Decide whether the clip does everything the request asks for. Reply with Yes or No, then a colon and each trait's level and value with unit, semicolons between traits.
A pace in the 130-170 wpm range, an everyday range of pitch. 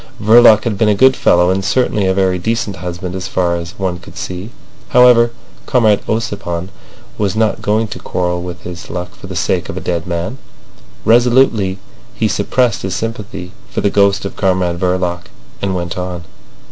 No: average, 180 wpm; average, 3.8 semitones